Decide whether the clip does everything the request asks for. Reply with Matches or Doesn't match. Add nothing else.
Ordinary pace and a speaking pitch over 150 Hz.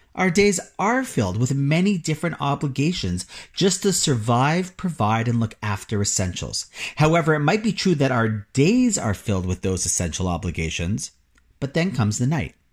Doesn't match